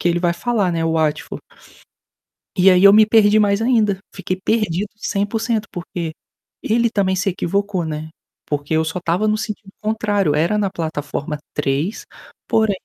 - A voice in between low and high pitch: No, high, 195 Hz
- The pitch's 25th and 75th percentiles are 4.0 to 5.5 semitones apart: Yes, average, 4.3 semitones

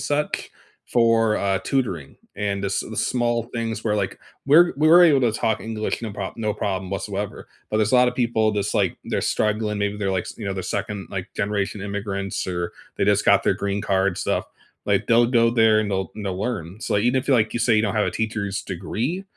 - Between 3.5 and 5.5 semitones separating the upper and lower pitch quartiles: No, average, 2.9 semitones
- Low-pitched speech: Yes, low, 105 Hz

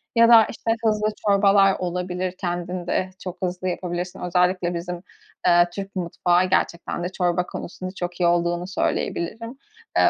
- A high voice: No, medium, 180 Hz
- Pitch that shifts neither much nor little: No, narrow, 1.6 semitones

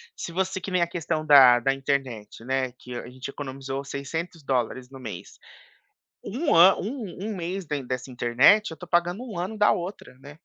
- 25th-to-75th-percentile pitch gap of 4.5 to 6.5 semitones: Yes, wide, 5.6 semitones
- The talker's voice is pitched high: No, medium, 145 Hz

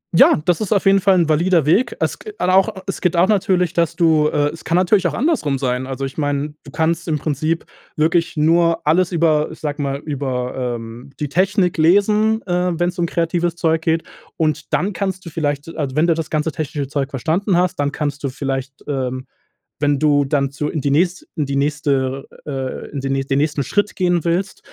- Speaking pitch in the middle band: Yes, medium, 155 Hz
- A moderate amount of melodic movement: Yes, average, 3.8 semitones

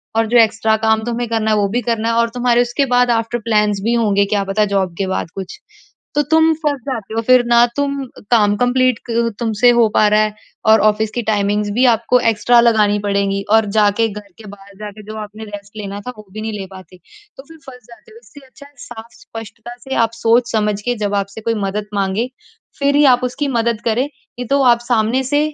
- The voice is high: Yes, high, 225 Hz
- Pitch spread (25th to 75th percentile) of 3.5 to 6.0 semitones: No, average, 2.8 semitones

